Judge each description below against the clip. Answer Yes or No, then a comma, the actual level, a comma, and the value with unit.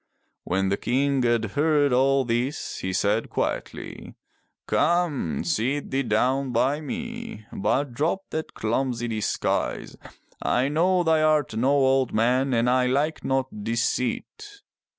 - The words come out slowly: Yes, slow, 130 wpm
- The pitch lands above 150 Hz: No, low, 135 Hz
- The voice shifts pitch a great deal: No, average, 4.2 semitones